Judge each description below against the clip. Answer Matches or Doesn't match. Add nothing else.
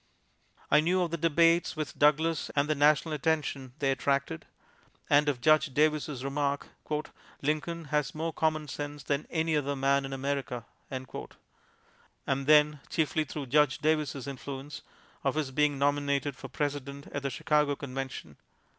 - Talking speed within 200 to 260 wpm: Doesn't match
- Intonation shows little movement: Matches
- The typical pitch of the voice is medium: Matches